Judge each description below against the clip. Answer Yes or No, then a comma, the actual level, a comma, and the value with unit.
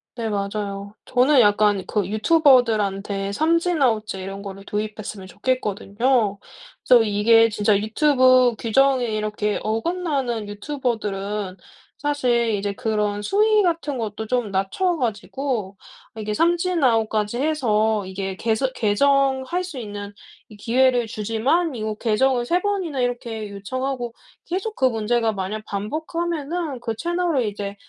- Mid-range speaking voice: No, high, 225 Hz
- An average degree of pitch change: Yes, average, 4.7 semitones